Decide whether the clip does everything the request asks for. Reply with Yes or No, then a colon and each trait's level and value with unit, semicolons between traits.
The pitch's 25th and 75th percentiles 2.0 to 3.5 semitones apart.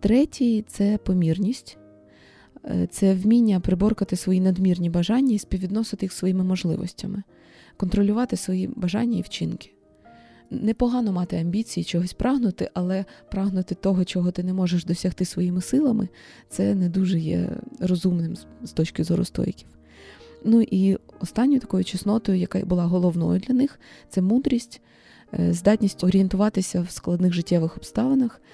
Yes: average, 3.2 semitones